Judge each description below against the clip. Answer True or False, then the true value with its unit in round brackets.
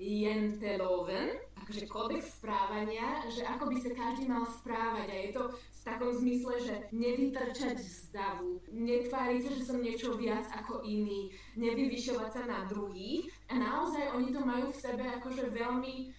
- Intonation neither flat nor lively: True (3.0 semitones)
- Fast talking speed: False (150 wpm)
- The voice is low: False (240 Hz)